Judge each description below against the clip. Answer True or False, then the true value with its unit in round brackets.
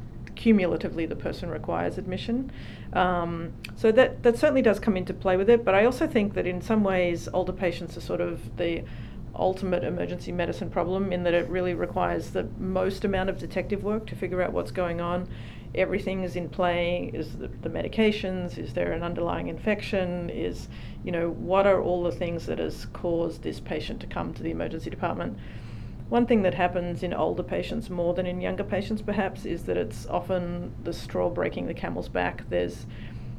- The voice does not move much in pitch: True (2.3 semitones)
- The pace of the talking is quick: False (190 wpm)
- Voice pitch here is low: False (180 Hz)